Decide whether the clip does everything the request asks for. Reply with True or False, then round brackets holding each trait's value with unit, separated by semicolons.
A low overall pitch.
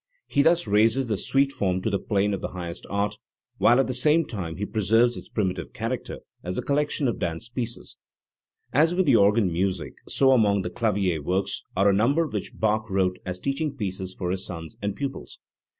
True (105 Hz)